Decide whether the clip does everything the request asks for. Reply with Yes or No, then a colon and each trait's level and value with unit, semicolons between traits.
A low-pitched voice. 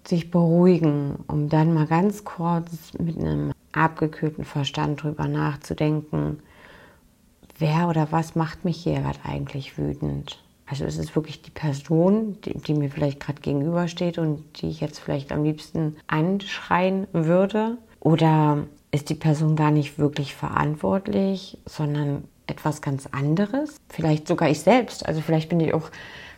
No: medium, 155 Hz